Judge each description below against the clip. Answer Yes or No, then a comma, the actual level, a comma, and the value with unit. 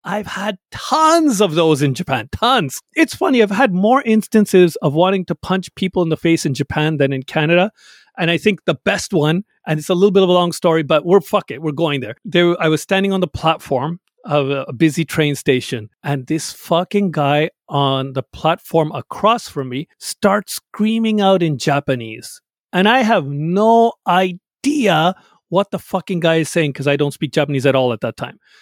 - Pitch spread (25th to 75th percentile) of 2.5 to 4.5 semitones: No, average, 5.1 semitones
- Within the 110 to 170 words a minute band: No, fast, 205 wpm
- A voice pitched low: No, medium, 170 Hz